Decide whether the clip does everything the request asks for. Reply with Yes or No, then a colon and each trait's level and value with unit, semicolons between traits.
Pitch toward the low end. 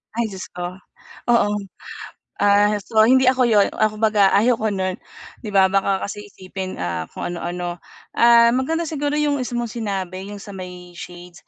No: high, 205 Hz